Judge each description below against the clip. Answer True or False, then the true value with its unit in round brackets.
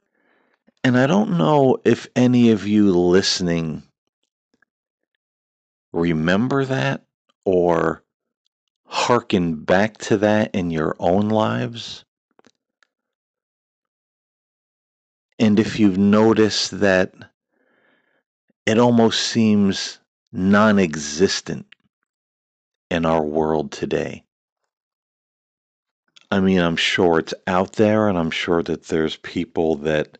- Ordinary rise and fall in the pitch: True (5.0 semitones)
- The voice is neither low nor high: False (95 Hz)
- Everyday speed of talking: False (95 wpm)